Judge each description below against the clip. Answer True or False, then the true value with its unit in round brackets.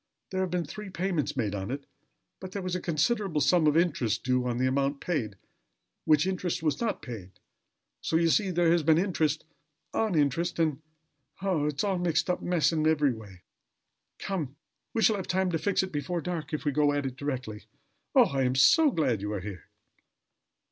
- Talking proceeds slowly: False (205 wpm)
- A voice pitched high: False (155 Hz)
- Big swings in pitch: False (4.9 semitones)